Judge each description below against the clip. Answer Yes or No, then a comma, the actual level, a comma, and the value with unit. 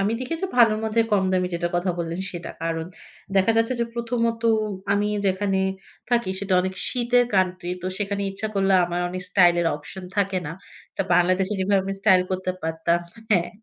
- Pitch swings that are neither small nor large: Yes, average, 3.2 semitones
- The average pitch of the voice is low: No, high, 190 Hz